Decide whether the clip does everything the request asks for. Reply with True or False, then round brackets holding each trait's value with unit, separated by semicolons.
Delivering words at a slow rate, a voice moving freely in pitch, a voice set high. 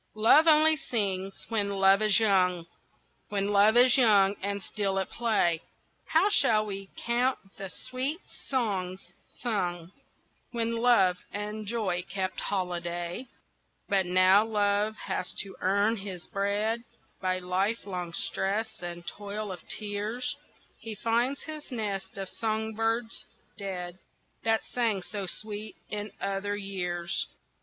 False (130 wpm; 3.0 semitones; 205 Hz)